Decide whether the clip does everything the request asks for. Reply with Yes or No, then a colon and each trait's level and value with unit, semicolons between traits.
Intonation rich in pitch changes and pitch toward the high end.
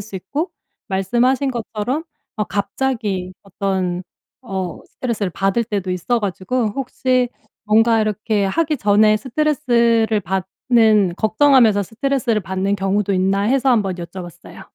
No: average, 4.1 semitones; high, 215 Hz